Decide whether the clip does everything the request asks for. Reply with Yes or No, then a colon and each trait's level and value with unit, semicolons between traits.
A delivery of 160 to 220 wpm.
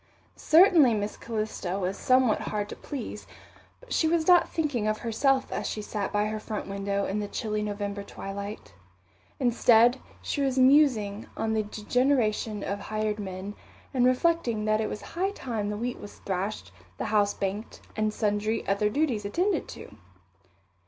Yes: average, 165 wpm